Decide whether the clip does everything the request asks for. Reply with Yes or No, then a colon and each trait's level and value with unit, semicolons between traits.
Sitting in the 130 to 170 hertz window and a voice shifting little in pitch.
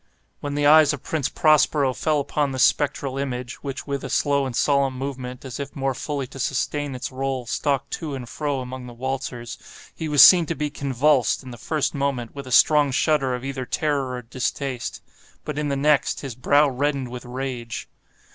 Yes: low, 135 Hz; narrow, 2.2 semitones